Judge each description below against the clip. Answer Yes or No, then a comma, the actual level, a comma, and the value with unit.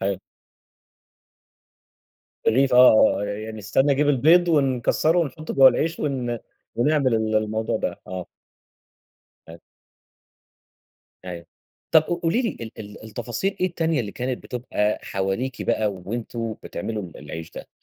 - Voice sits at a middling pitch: No, low, 120 Hz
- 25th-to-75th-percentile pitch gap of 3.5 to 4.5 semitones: No, wide, 5.4 semitones